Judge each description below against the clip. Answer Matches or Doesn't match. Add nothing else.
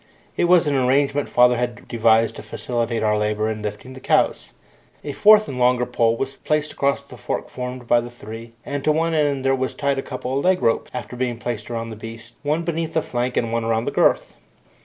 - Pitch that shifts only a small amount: Doesn't match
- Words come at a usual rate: Doesn't match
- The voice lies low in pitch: Matches